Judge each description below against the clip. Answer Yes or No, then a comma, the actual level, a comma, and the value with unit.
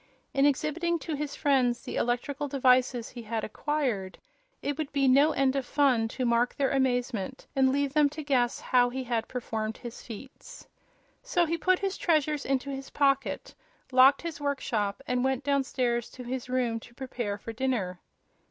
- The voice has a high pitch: Yes, very high, 265 Hz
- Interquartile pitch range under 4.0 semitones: Yes, average, 2.8 semitones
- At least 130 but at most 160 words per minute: No, average, 170 wpm